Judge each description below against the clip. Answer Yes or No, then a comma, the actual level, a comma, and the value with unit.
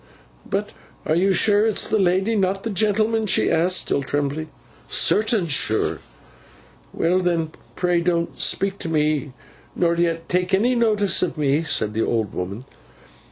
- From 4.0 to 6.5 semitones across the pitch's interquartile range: Yes, average, 4.4 semitones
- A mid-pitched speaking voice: Yes, medium, 175 Hz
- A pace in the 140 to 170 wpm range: Yes, average, 160 wpm